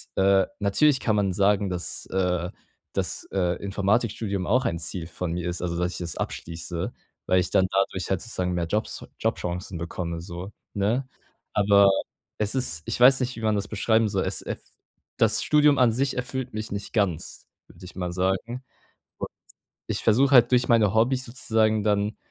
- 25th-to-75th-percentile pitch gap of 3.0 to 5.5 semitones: Yes, average, 4.2 semitones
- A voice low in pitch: Yes, low, 100 Hz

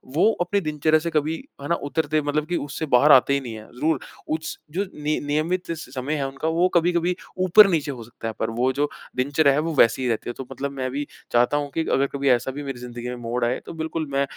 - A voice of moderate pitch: Yes, medium, 145 Hz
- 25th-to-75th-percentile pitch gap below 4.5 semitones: Yes, average, 3.6 semitones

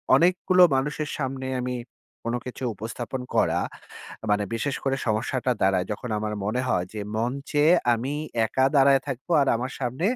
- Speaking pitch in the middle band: No, low, 125 Hz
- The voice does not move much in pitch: No, average, 3.4 semitones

